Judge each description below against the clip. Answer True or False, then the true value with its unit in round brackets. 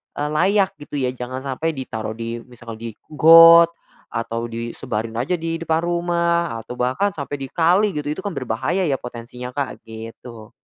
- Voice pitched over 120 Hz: True (135 Hz)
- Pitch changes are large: True (6.2 semitones)